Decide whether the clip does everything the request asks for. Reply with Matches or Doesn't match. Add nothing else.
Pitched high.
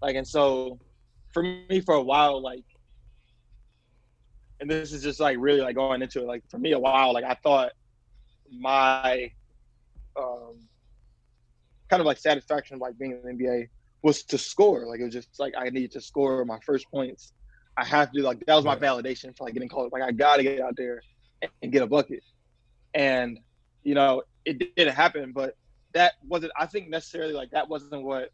Doesn't match